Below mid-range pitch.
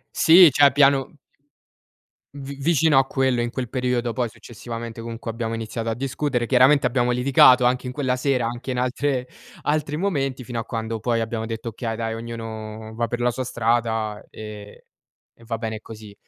Yes: low, 120 Hz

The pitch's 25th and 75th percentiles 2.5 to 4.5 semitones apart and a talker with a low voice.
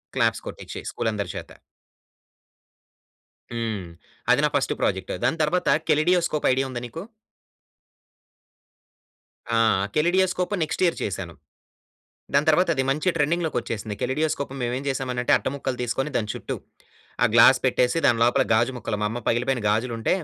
No: average, 4.9 semitones; low, 130 Hz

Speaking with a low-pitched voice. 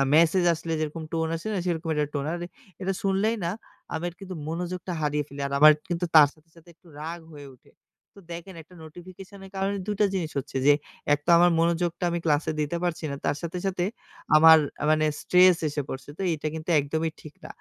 No: medium, 165 Hz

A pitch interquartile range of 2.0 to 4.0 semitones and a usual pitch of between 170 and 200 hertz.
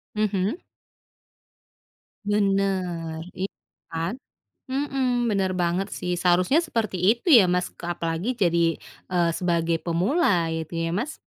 Yes: average, 3.7 semitones; medium, 185 Hz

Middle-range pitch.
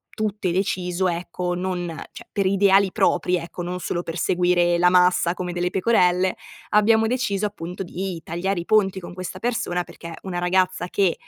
Yes: medium, 180 Hz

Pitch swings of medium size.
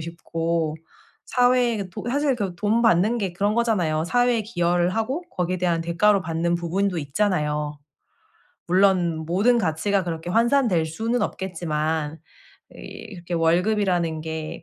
Yes: average, 4.7 semitones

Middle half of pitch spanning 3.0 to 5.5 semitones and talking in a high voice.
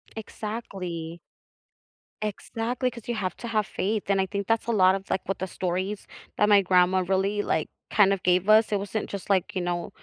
No: narrow, 2.6 semitones; high, 195 Hz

